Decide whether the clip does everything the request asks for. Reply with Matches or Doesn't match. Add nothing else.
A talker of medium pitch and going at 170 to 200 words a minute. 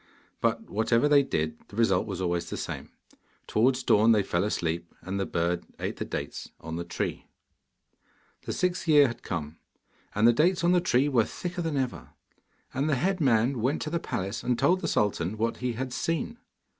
Doesn't match